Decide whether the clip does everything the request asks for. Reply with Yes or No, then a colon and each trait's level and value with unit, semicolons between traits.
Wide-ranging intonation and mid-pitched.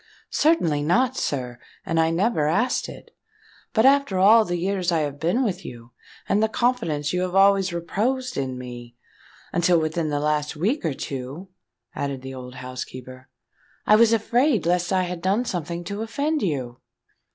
Yes: wide, 6.8 semitones; medium, 175 Hz